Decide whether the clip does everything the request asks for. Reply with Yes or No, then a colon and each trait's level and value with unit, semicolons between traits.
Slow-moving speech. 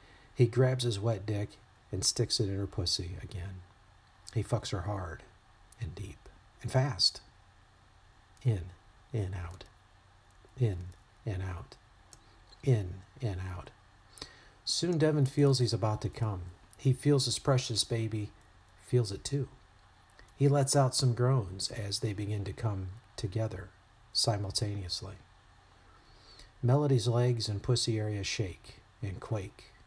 Yes: slow, 130 wpm